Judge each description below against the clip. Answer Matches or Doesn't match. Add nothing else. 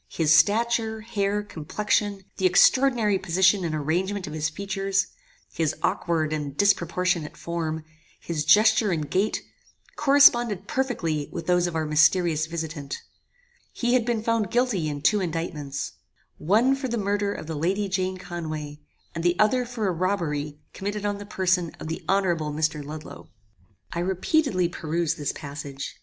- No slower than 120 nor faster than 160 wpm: Matches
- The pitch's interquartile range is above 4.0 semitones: Matches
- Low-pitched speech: Doesn't match